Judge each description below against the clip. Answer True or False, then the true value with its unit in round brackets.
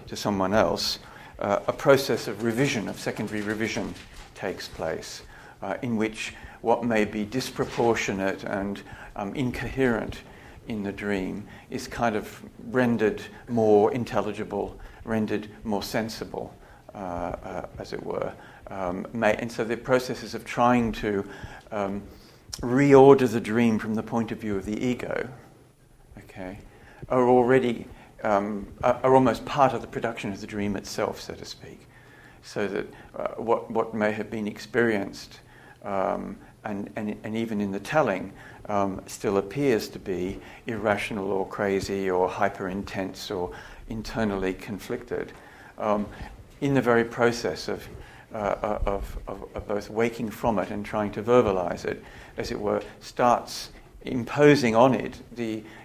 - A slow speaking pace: False (145 wpm)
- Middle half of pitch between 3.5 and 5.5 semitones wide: False (3.0 semitones)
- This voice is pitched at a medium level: False (110 Hz)